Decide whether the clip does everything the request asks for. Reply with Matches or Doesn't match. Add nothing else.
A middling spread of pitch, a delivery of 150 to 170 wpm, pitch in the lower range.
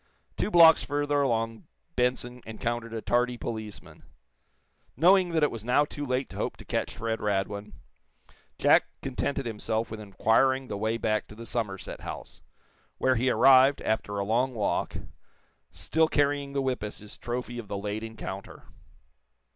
Matches